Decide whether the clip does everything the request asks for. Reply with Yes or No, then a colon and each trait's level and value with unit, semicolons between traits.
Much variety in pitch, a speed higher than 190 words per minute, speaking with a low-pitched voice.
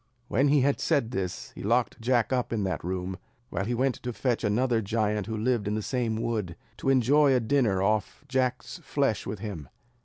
No: average, 3.7 semitones; fast, 205 wpm; low, 115 Hz